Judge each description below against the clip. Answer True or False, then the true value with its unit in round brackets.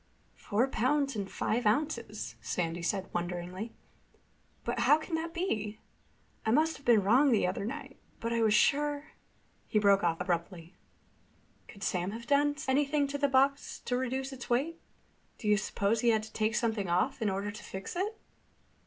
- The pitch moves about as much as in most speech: False (5.7 semitones)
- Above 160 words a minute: True (175 wpm)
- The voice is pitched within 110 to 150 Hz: False (230 Hz)